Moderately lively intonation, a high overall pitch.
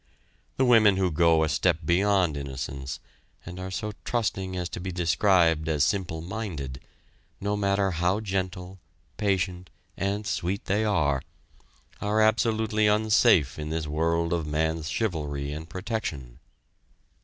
No: average, 4.3 semitones; very low, 90 Hz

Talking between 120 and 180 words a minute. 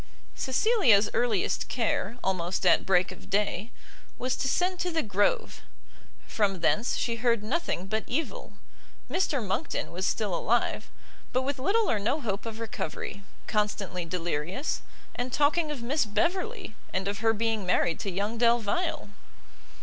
Yes: average, 150 wpm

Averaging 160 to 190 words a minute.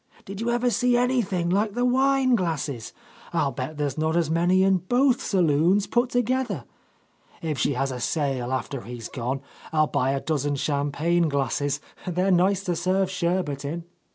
Yes: average, 175 wpm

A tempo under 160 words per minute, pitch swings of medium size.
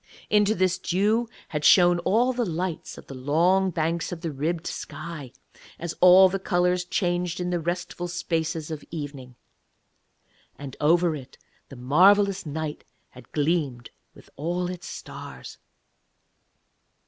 Yes: slow, 135 wpm; average, 3.1 semitones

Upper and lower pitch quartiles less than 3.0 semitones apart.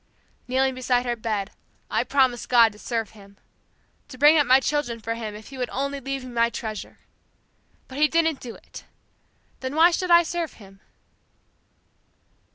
No: average, 3.7 semitones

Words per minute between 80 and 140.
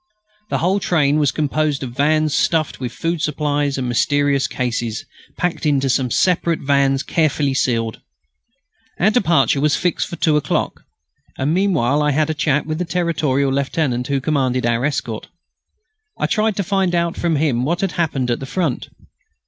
No: average, 170 wpm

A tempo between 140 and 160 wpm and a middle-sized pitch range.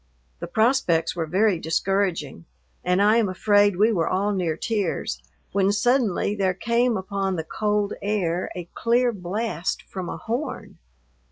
Yes: average, 150 wpm; average, 3.5 semitones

